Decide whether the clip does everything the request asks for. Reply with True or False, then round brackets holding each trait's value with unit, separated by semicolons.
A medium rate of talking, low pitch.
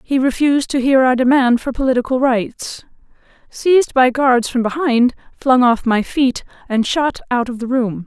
False (180 wpm; 255 Hz)